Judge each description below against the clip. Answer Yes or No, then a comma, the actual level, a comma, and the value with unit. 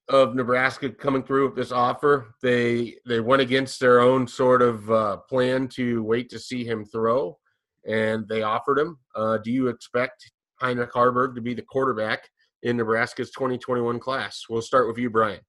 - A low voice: Yes, low, 125 Hz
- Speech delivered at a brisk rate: No, average, 185 wpm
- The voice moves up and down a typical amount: No, narrow, 2.3 semitones